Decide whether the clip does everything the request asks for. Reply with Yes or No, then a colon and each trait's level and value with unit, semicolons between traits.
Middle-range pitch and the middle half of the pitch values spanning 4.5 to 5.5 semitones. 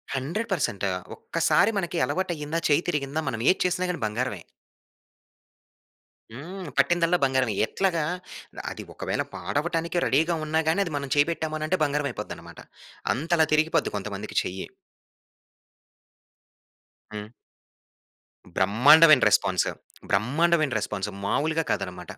Yes: medium, 155 Hz; average, 4.9 semitones